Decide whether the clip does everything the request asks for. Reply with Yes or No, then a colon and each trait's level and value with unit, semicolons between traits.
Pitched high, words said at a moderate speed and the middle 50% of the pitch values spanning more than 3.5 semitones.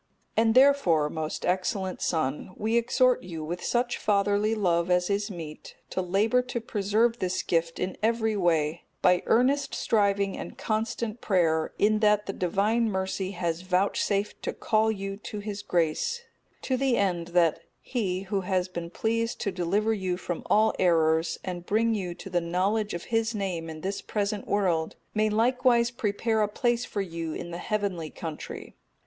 Yes: high, 200 Hz; average, 170 wpm; average, 3.9 semitones